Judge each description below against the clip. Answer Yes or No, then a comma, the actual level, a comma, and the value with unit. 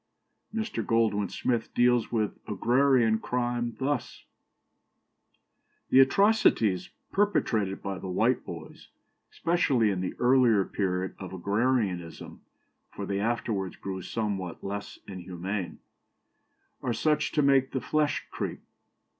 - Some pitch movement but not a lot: Yes, average, 5.0 semitones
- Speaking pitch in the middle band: No, low, 115 Hz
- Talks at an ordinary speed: No, slow, 115 wpm